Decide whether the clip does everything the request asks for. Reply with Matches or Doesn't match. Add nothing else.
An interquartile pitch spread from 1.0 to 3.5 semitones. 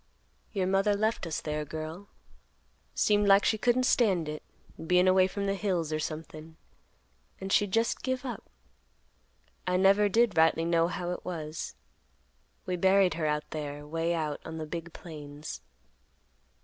Doesn't match